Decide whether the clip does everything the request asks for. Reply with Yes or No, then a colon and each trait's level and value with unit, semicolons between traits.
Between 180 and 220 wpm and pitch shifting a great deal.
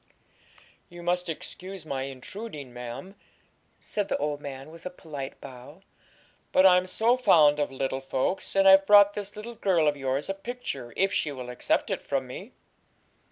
No: average, 170 wpm; wide, 6.2 semitones